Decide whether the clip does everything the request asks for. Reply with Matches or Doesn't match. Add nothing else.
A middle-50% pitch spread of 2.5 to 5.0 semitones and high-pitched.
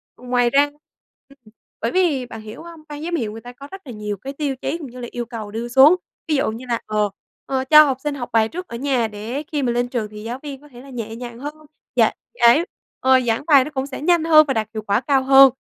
Matches